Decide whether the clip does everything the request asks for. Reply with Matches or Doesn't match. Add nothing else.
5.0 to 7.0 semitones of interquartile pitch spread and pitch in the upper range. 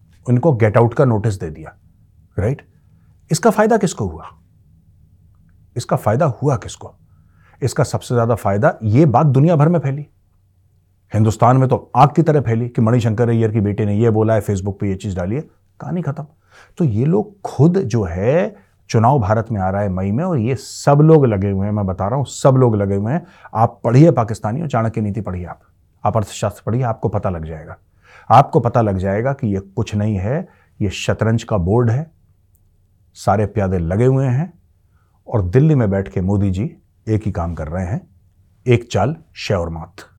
Doesn't match